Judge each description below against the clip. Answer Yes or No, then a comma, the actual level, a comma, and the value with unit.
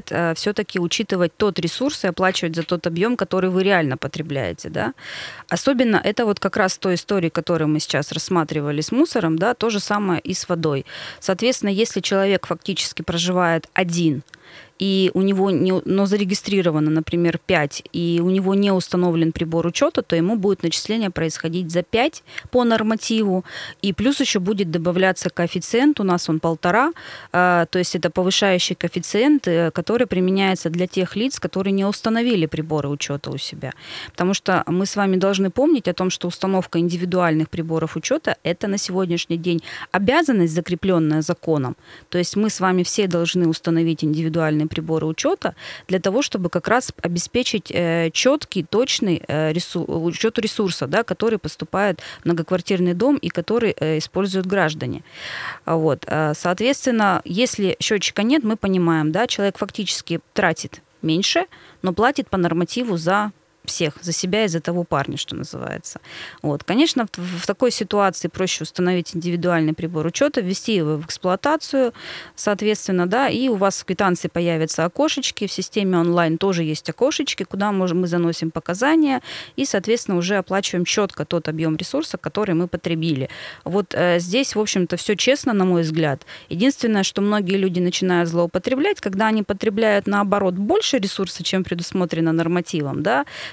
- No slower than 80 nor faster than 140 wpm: No, average, 155 wpm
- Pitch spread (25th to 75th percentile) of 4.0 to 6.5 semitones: No, average, 3.6 semitones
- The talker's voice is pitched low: No, medium, 185 Hz